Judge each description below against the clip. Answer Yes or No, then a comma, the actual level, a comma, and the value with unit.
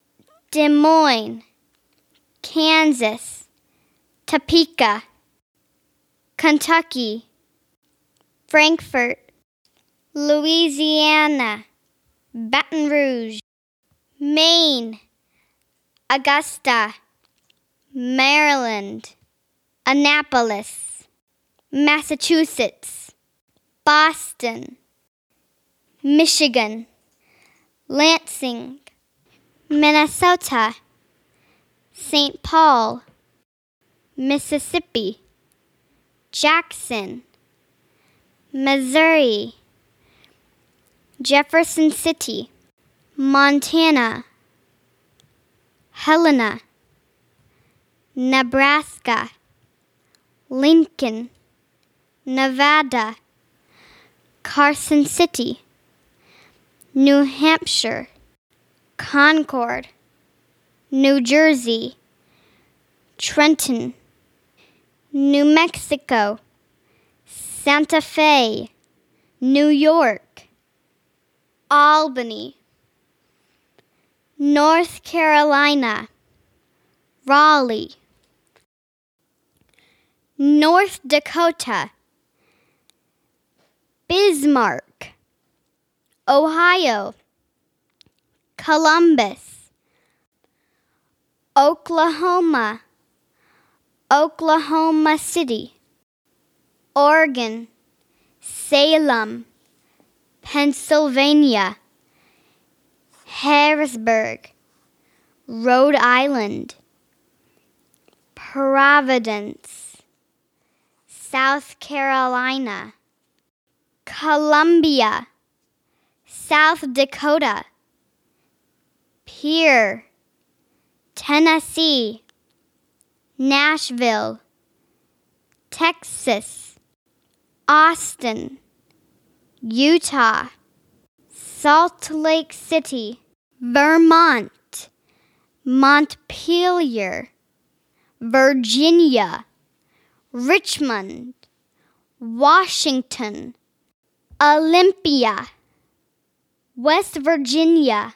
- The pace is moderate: No, slow, 35 wpm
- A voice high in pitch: Yes, very high, 290 Hz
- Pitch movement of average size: Yes, average, 3.5 semitones